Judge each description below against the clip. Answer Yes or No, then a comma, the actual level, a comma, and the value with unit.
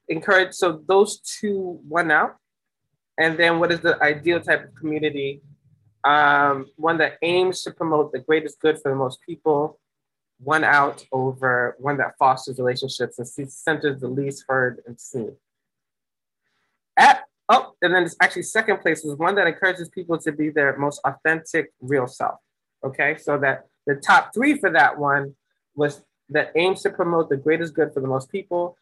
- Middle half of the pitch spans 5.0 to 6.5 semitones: No, average, 3.7 semitones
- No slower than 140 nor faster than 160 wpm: No, average, 175 wpm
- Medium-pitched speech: Yes, medium, 150 Hz